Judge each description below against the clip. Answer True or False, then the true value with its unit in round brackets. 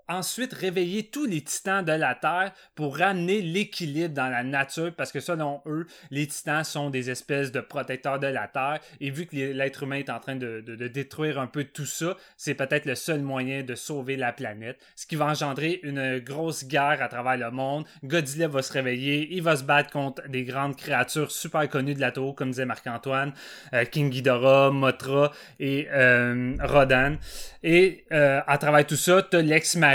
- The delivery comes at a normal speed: True (200 wpm)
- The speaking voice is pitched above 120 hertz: True (140 Hz)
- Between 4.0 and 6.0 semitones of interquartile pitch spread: False (2.8 semitones)